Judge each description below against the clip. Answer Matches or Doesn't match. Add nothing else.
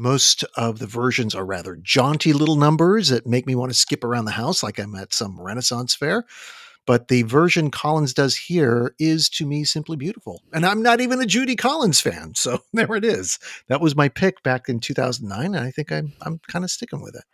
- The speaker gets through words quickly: Matches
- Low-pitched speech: Doesn't match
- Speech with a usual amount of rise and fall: Doesn't match